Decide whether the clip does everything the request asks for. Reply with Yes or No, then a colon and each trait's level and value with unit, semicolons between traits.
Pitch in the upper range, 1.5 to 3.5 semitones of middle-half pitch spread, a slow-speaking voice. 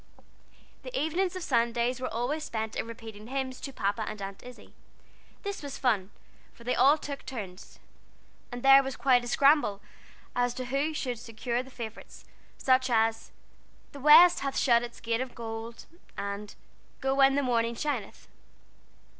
No: high, 245 Hz; average, 3.2 semitones; average, 165 wpm